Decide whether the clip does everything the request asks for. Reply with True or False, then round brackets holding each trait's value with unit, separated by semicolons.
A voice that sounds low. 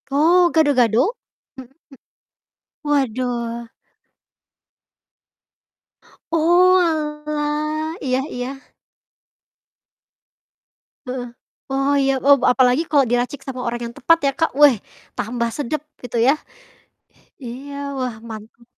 False (270 Hz)